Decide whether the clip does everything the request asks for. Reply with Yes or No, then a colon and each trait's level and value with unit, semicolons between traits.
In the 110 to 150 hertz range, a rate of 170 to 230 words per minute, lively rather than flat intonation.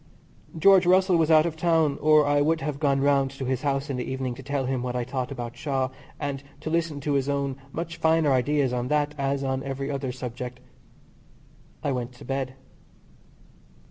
No: medium, 140 Hz; average, 200 wpm; average, 2.7 semitones